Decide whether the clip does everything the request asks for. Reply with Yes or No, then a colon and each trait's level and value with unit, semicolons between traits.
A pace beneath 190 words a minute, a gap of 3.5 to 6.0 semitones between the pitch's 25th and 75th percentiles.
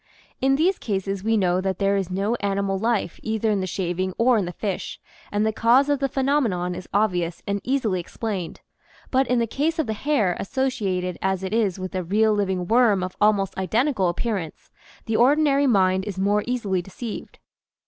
No: average, 195 wpm; average, 4.1 semitones